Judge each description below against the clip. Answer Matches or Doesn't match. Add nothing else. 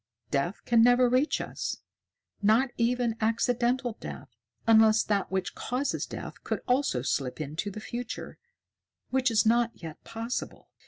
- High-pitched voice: Matches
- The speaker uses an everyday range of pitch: Matches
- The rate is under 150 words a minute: Matches